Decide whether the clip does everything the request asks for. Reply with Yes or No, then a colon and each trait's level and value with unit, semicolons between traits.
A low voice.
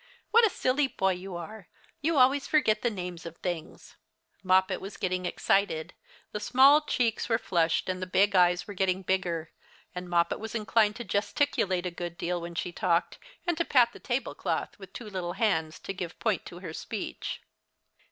No: high, 190 Hz